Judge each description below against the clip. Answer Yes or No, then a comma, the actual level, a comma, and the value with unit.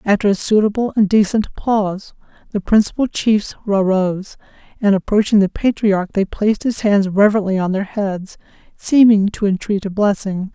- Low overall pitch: No, high, 205 Hz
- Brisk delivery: No, average, 155 wpm